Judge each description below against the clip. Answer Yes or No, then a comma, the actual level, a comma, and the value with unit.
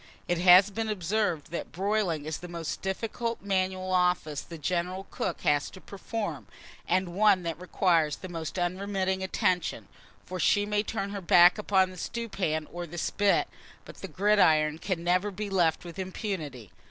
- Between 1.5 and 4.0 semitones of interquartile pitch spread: Yes, average, 2.8 semitones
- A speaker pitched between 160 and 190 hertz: Yes, medium, 185 Hz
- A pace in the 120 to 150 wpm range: No, average, 165 wpm